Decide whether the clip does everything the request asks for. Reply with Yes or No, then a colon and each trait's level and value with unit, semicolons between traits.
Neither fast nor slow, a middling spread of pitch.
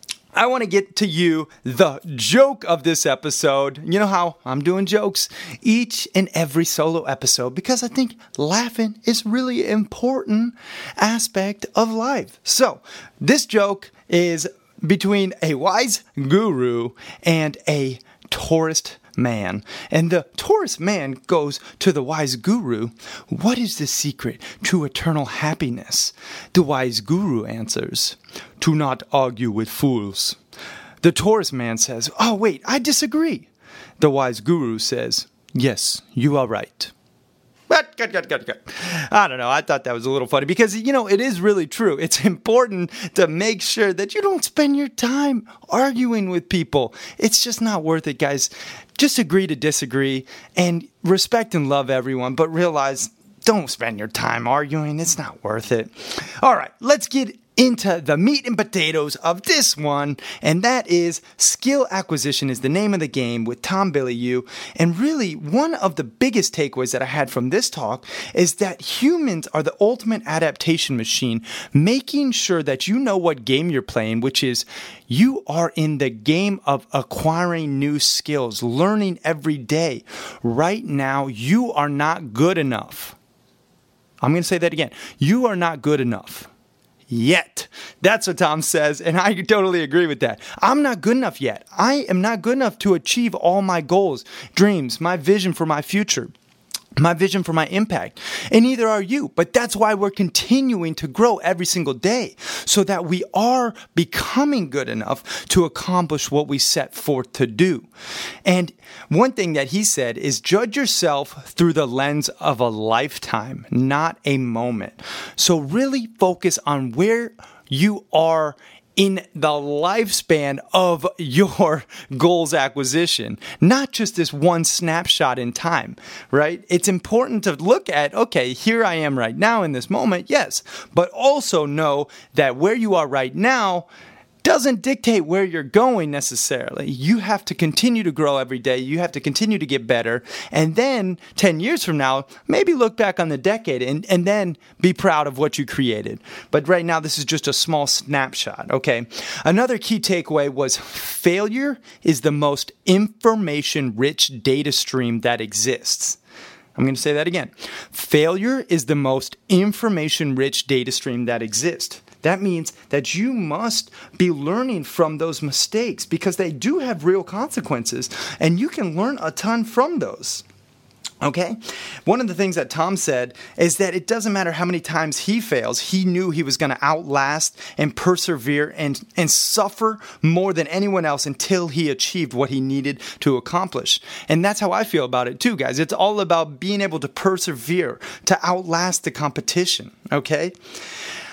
No: average, 165 wpm; wide, 6.5 semitones